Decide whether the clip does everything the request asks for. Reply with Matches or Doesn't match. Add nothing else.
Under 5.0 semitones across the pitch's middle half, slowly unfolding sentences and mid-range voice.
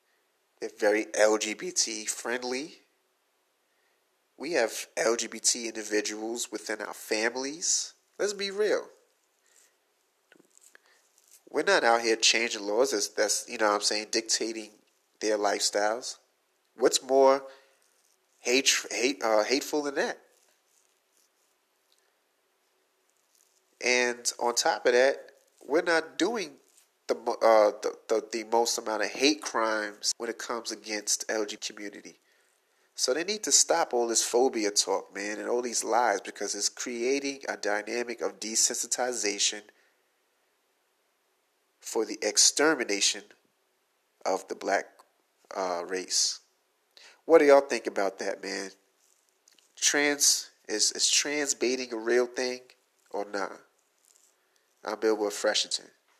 Doesn't match